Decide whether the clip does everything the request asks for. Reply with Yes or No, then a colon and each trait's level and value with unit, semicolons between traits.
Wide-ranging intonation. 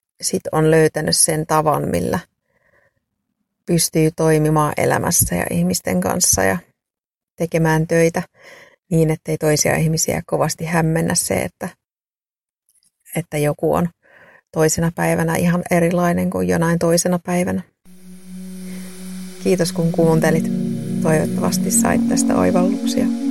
No: average, 2.8 semitones